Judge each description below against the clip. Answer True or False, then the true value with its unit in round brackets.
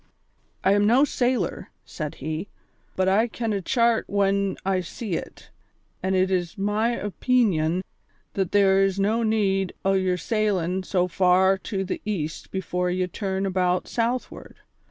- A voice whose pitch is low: False (195 Hz)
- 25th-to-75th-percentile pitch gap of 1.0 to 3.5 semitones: True (2.6 semitones)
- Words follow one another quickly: False (155 wpm)